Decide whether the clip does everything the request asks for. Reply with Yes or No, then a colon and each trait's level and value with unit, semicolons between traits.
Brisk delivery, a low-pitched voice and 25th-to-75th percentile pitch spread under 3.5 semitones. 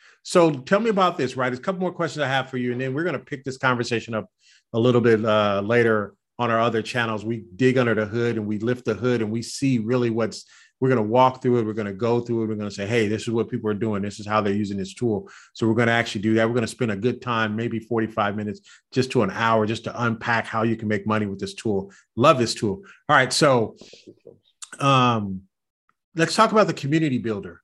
Yes: fast, 265 wpm; low, 115 Hz; narrow, 2.6 semitones